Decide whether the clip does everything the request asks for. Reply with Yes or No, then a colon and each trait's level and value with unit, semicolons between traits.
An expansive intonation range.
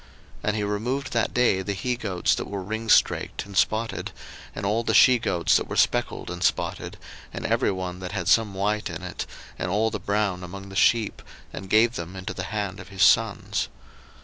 No: average, 2.9 semitones